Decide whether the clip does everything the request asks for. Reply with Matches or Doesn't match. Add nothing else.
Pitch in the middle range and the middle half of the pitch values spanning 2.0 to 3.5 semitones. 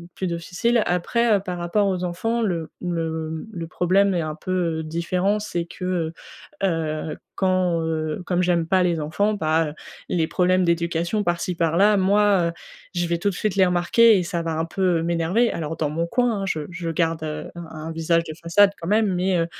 Matches